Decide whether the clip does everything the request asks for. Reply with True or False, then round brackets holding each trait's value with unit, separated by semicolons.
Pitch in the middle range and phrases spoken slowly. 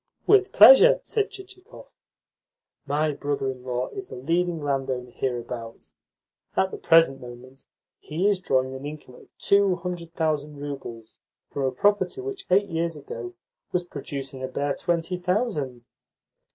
False (155 Hz; 145 wpm)